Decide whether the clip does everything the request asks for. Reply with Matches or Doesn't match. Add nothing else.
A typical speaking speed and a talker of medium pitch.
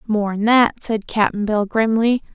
Doesn't match